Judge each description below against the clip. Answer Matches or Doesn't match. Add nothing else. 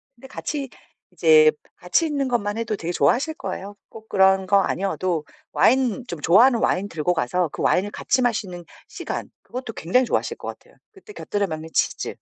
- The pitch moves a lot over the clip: Matches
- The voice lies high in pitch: Matches